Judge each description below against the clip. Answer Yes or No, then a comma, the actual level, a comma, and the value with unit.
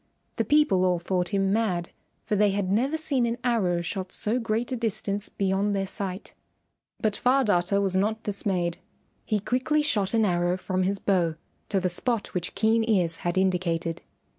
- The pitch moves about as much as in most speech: Yes, average, 3.5 semitones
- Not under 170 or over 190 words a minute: Yes, average, 180 wpm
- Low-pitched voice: No, high, 200 Hz